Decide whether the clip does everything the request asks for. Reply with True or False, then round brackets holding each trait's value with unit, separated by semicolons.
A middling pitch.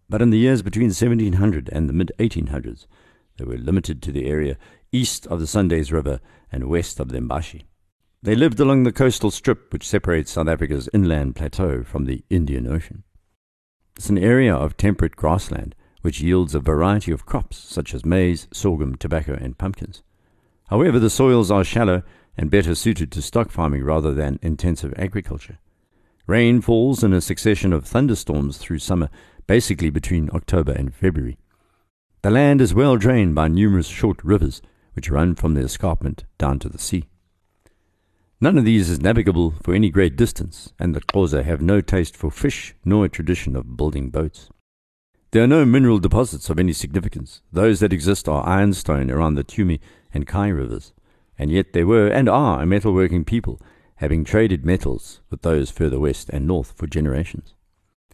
False (90 Hz)